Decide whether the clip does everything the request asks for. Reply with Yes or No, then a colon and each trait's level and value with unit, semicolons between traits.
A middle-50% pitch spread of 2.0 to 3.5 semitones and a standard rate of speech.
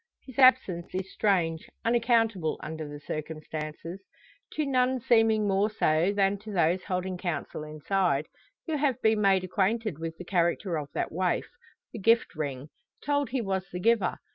No: wide, 5.5 semitones; average, 160 wpm